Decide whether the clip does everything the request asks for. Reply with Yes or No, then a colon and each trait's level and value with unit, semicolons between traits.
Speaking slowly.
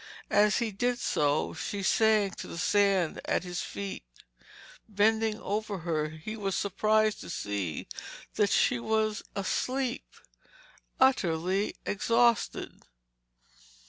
Yes: slow, 110 wpm